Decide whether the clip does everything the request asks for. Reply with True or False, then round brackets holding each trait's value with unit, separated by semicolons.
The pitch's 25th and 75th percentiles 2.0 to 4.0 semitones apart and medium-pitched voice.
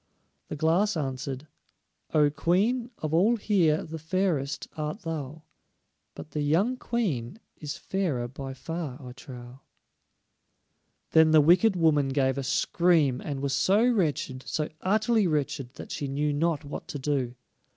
False (4.6 semitones; 155 Hz)